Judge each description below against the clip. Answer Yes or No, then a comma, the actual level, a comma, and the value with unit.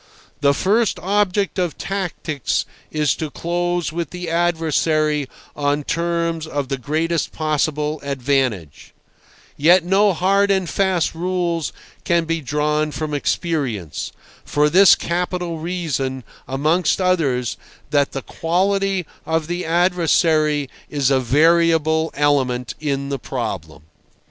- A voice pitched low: No, medium, 160 Hz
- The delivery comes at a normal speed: No, slow, 115 wpm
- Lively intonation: No, average, 3.6 semitones